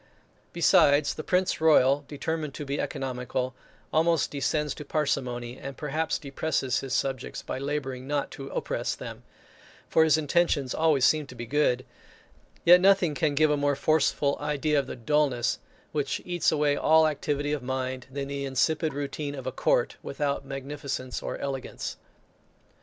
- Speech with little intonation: Yes, narrow, 2.3 semitones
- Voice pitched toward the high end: No, medium, 145 Hz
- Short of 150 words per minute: No, average, 160 wpm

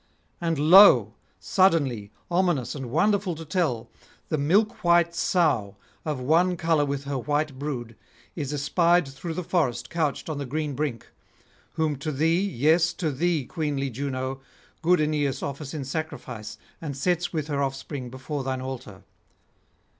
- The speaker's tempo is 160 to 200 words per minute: No, average, 150 wpm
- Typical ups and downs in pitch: Yes, average, 4.0 semitones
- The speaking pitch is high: No, medium, 150 Hz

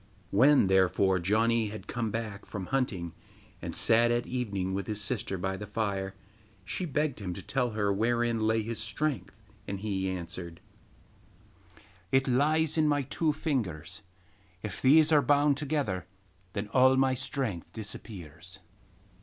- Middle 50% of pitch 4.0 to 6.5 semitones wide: Yes, wide, 5.5 semitones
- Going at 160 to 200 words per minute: No, average, 145 wpm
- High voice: No, low, 110 Hz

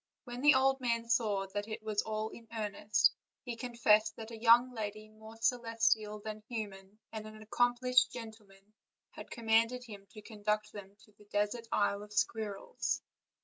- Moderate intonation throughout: No, narrow, 1.9 semitones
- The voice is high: Yes, high, 220 Hz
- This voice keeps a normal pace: Yes, average, 175 wpm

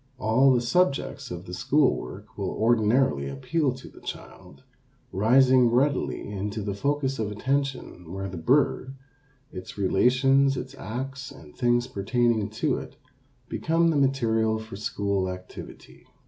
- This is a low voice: Yes, low, 120 Hz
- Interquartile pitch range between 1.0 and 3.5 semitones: No, average, 4.9 semitones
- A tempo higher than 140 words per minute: No, slow, 135 wpm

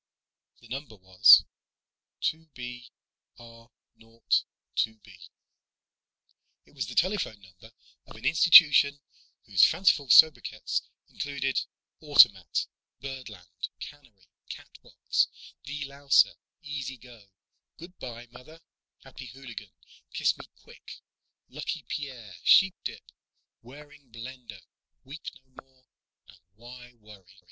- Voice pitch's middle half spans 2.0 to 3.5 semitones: No, average, 4.3 semitones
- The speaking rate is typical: No, slow, 105 wpm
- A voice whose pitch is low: Yes, low, 125 Hz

